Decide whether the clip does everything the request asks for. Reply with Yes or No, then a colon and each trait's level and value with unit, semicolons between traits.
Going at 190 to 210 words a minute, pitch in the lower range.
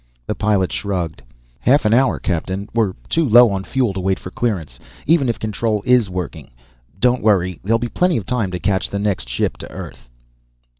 Yes: average, 195 wpm; low, 100 Hz